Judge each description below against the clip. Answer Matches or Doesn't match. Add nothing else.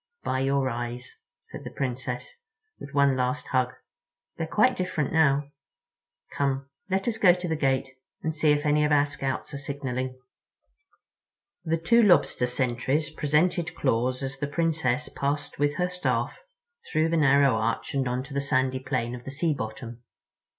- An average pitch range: Matches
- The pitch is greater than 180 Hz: Doesn't match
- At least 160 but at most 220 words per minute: Matches